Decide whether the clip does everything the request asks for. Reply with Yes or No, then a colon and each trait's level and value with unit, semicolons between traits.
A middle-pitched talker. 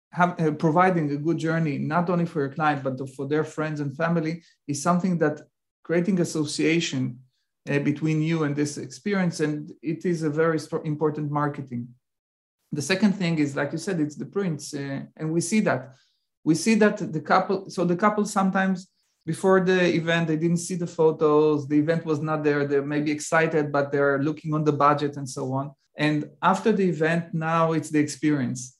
Yes: medium, 155 Hz